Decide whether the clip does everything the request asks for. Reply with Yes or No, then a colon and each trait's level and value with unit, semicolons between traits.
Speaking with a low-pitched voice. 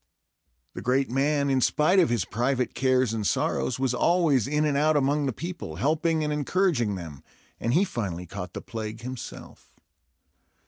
Yes: low, 130 Hz